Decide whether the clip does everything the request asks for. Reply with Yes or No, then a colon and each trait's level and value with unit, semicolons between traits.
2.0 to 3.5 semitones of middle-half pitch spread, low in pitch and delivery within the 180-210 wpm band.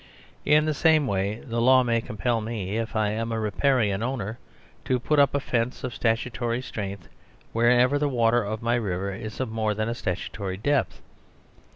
Yes: average, 3.0 semitones; low, 115 Hz; average, 185 wpm